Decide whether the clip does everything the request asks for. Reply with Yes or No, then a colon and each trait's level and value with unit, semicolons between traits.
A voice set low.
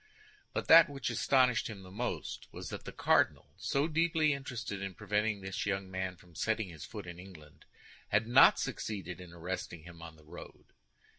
Yes: low, 100 Hz